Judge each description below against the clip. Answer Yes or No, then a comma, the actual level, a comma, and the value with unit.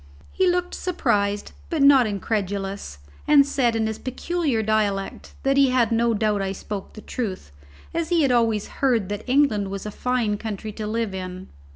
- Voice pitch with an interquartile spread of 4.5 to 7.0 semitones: Yes, average, 4.8 semitones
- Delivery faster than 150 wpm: Yes, average, 180 wpm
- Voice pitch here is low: No, high, 220 Hz